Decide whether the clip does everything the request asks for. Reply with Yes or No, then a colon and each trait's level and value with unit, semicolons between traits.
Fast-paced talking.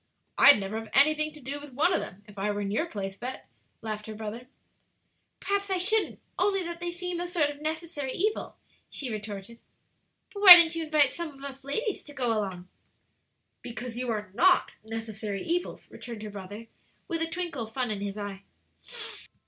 No: average, 195 wpm